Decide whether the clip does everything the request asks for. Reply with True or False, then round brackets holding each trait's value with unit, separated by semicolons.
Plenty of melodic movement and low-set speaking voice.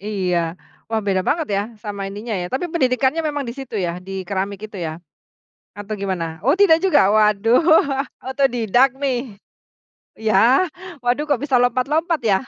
False (5.7 semitones; 230 Hz)